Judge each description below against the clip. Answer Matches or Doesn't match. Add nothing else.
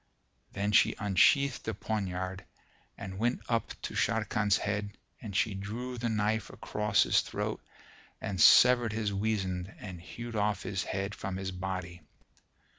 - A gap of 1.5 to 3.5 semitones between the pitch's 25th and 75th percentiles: Matches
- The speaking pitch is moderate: Doesn't match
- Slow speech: Doesn't match